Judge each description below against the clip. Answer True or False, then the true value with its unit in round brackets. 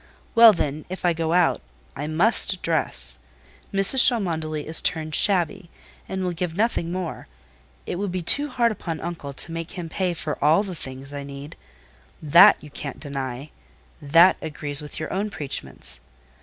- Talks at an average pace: True (165 wpm)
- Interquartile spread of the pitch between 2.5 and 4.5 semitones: True (4.0 semitones)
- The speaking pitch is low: False (165 Hz)